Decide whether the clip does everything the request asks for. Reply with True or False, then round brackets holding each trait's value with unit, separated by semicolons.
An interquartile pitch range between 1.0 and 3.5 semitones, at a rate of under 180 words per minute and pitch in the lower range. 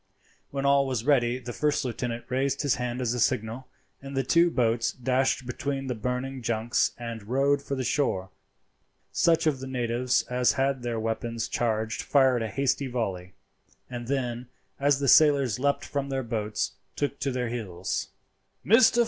True (2.8 semitones; 170 wpm; 125 Hz)